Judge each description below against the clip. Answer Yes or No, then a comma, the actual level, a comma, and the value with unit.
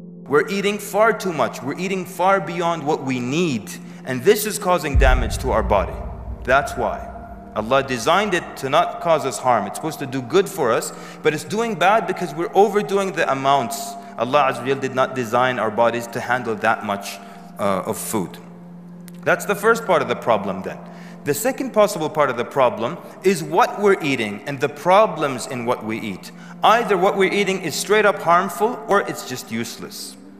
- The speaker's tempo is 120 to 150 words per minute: No, average, 195 wpm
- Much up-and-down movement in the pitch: Yes, wide, 7.0 semitones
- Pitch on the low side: No, medium, 175 Hz